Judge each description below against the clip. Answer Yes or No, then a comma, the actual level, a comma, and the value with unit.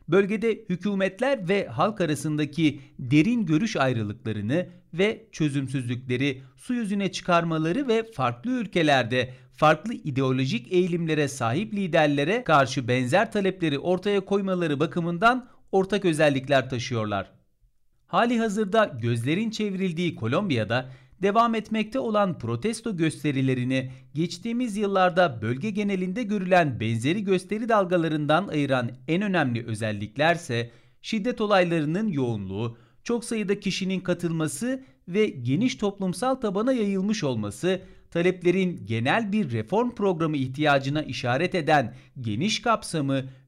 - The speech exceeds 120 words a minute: No, average, 105 wpm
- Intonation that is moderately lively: No, wide, 7.5 semitones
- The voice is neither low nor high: Yes, medium, 170 Hz